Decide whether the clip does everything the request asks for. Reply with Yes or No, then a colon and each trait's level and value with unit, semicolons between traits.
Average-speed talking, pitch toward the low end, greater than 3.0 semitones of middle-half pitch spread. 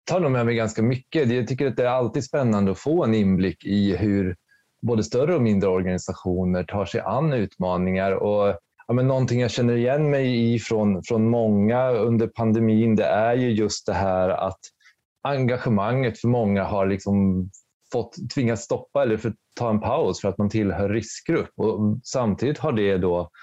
Yes: average, 185 wpm; low, 110 Hz; average, 3.6 semitones